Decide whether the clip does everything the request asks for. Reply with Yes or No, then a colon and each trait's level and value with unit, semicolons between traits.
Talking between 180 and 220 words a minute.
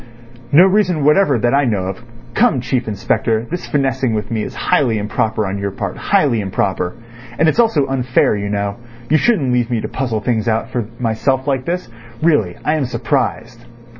Yes: average, 185 wpm